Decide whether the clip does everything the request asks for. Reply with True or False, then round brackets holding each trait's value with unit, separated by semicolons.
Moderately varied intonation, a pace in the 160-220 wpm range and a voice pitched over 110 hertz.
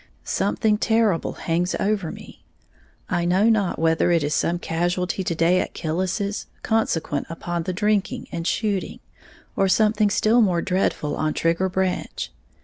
False (3.8 semitones; 145 wpm; 185 Hz)